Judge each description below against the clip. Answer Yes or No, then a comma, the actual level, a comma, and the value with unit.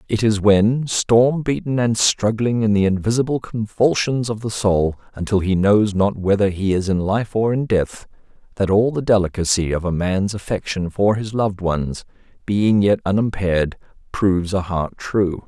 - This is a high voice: No, low, 105 Hz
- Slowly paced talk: No, average, 175 wpm